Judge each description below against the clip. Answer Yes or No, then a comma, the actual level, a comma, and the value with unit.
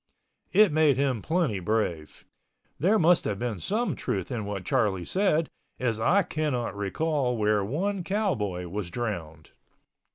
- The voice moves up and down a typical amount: No, wide, 8.2 semitones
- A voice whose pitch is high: No, low, 120 Hz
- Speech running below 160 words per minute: Yes, average, 140 wpm